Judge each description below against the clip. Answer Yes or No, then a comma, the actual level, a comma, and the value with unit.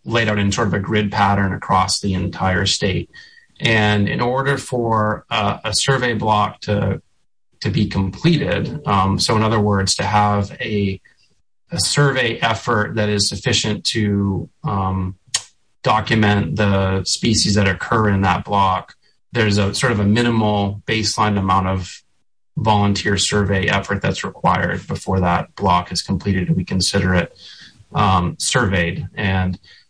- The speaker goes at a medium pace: Yes, average, 150 wpm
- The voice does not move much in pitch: Yes, narrow, 2.1 semitones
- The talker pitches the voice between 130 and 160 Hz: No, low, 100 Hz